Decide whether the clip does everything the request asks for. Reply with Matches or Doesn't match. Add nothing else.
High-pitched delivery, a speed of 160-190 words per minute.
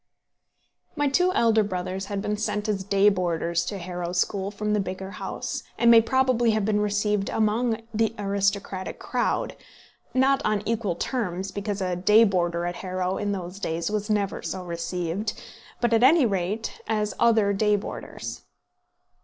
Matches